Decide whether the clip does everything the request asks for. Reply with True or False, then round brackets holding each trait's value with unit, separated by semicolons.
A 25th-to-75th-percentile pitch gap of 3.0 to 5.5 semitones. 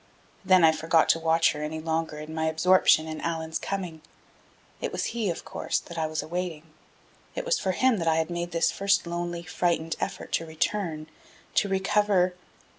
False (2.5 semitones)